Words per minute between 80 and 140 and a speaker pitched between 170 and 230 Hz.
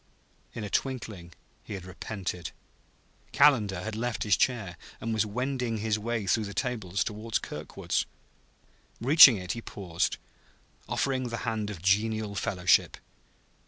No: slow, 135 wpm; low, 110 Hz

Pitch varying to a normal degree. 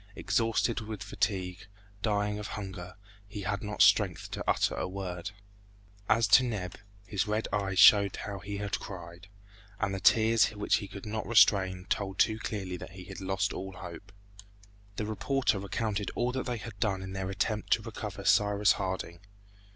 No: narrow, 2.1 semitones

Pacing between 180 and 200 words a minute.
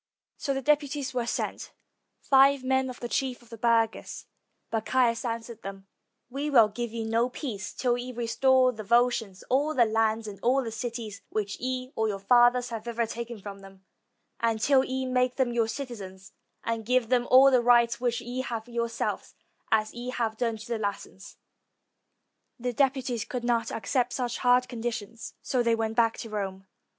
Yes: average, 185 wpm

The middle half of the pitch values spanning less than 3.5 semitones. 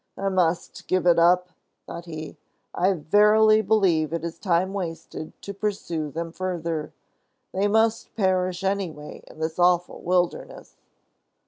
Yes: average, 2.8 semitones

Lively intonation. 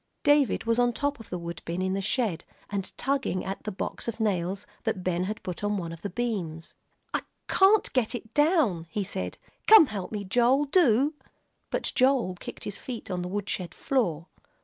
Yes: wide, 5.8 semitones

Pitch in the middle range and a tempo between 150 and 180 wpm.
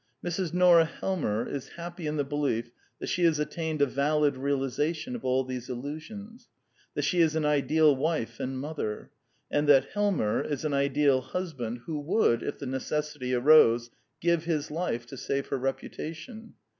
Yes: medium, 150 Hz; average, 170 wpm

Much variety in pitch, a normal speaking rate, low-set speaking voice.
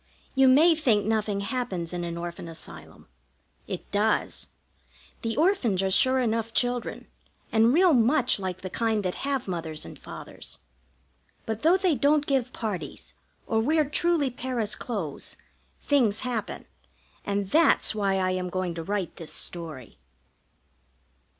No: wide, 6.0 semitones; average, 145 wpm; high, 220 Hz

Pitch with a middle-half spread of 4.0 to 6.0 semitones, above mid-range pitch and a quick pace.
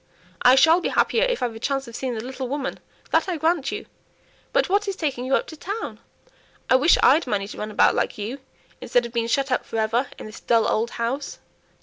Yes: average, 5.0 semitones; very high, 260 Hz; fast, 235 wpm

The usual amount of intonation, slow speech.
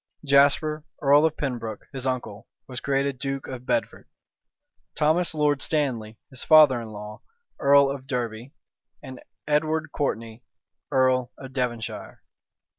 Yes: average, 3.1 semitones; slow, 125 wpm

